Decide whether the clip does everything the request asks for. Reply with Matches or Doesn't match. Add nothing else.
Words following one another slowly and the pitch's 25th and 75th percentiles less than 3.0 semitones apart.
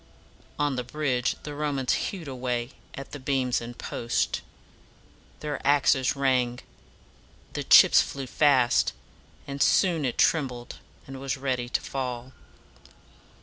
Matches